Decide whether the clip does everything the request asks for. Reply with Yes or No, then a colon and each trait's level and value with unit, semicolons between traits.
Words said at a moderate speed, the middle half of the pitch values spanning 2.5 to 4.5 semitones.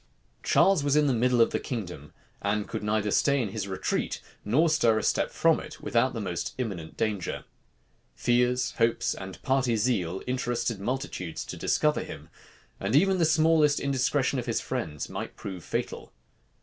No: average, 170 wpm; average, 4.9 semitones